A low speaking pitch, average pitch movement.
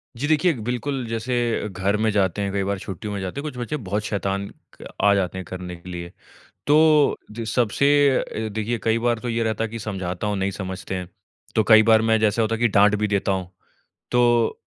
Yes: low, 105 Hz; average, 3.3 semitones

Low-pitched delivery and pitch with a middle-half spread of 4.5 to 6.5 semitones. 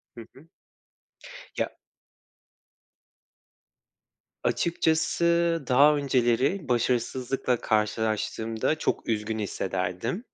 Yes: low, 125 Hz; wide, 5.4 semitones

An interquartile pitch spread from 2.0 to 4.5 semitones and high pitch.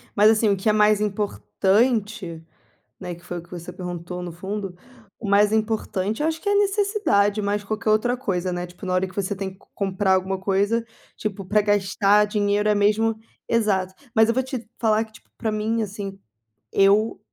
Yes: narrow, 2.4 semitones; high, 205 Hz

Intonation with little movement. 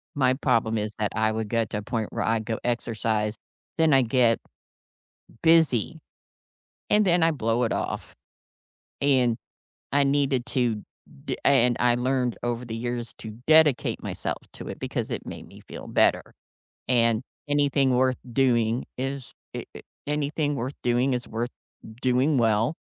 No: average, 3.3 semitones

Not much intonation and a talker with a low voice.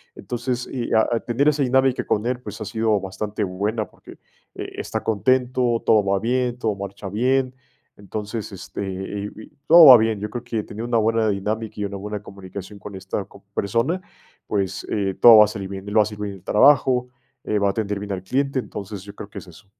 No: average, 3.3 semitones; low, 105 Hz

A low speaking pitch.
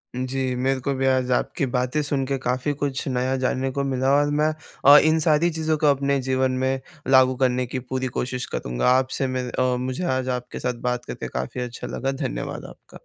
Yes: low, 130 Hz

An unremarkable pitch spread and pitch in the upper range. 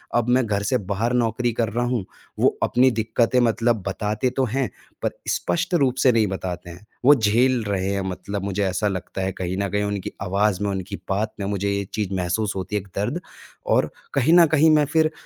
No: average, 4.0 semitones; low, 105 Hz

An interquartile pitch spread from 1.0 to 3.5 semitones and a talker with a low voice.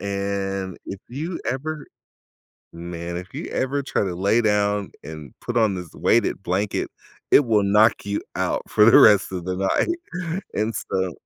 No: average, 4.0 semitones; low, 100 Hz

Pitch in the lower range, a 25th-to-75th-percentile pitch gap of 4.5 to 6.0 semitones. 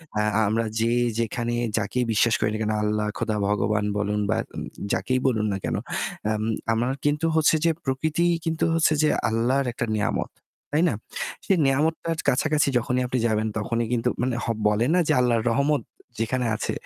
Yes: low, 120 Hz; average, 5.0 semitones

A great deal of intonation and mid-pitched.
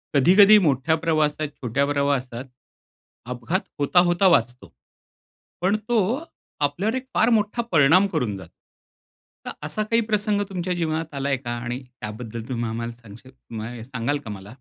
Yes: wide, 7.0 semitones; medium, 145 Hz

